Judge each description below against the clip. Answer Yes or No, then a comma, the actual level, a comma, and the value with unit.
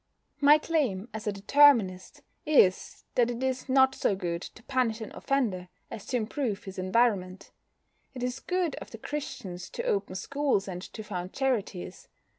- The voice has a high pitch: Yes, high, 225 Hz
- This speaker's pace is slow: No, average, 165 wpm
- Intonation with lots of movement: Yes, wide, 5.9 semitones